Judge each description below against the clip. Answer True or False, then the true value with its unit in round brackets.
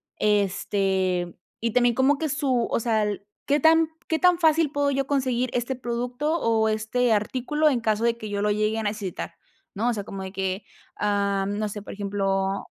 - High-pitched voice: True (220 Hz)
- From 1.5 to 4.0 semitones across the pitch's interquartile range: False (4.4 semitones)